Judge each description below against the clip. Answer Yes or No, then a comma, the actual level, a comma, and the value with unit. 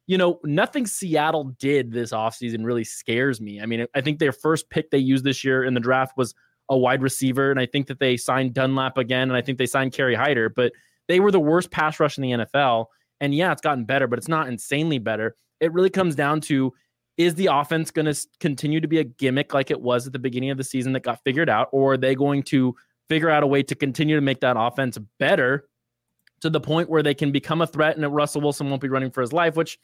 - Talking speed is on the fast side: Yes, fast, 255 wpm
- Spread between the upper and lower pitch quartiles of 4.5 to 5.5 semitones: No, average, 3.3 semitones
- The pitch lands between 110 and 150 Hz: Yes, low, 135 Hz